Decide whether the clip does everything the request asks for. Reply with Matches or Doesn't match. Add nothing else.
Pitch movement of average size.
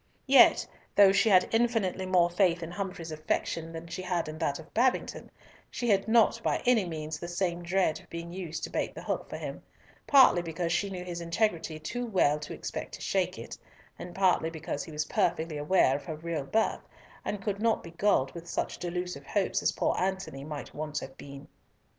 Matches